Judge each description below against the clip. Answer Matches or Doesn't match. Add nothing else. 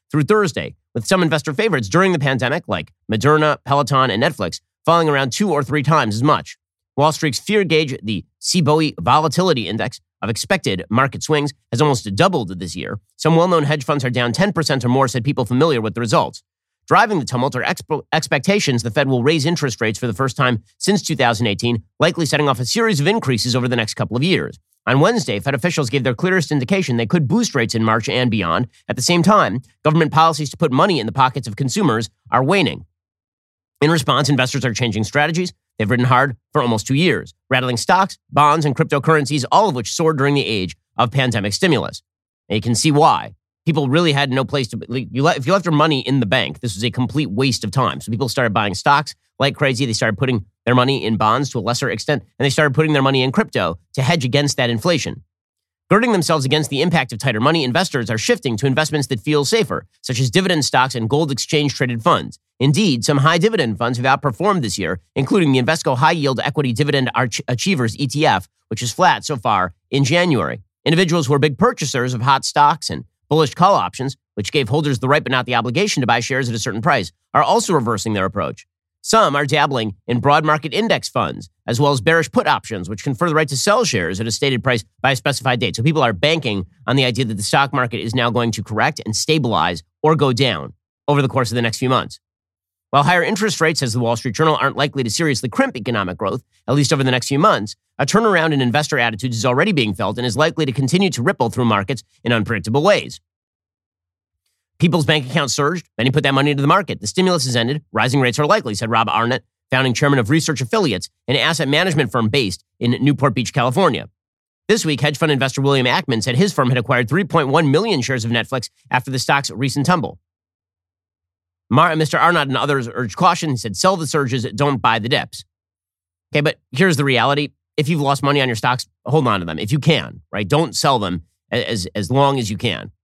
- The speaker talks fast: Matches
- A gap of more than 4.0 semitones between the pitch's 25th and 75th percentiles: Matches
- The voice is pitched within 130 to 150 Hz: Matches